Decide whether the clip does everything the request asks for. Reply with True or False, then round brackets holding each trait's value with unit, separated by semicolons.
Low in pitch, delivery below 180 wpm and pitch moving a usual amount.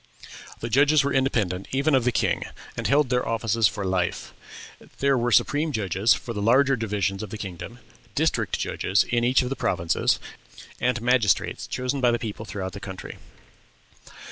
True (115 Hz; 170 wpm; 4.3 semitones)